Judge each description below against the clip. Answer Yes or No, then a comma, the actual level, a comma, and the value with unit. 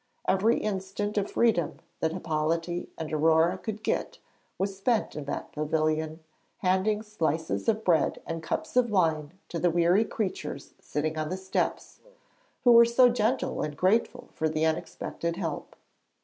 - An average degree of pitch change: Yes, average, 4.9 semitones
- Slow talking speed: No, average, 150 wpm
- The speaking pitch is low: No, medium, 175 Hz